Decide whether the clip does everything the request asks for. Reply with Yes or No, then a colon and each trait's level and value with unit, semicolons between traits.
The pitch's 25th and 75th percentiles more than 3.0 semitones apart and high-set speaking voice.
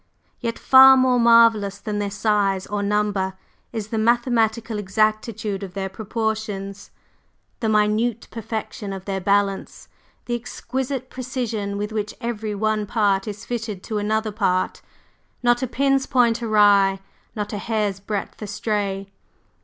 No: narrow, 2.5 semitones; high, 215 Hz